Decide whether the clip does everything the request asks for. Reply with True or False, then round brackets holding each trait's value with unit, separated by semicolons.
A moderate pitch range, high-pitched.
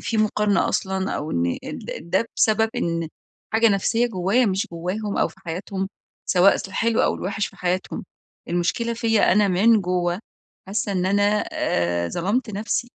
True (3.4 semitones; 195 Hz)